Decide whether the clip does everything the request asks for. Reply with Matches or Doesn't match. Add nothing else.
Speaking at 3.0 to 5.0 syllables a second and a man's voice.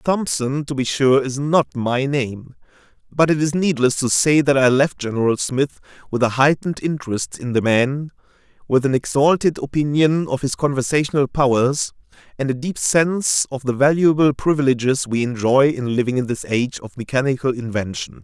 Doesn't match